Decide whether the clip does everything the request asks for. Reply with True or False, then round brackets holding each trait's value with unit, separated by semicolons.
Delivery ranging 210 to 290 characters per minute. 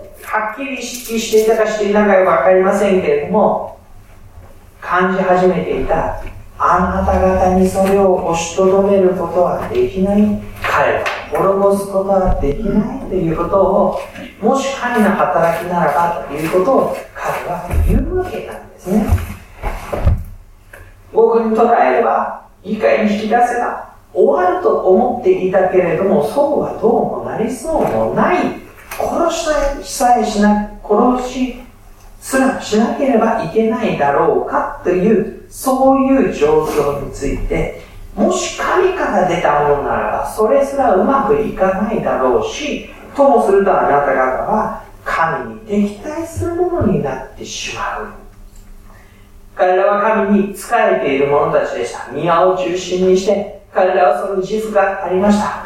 True (285 characters per minute)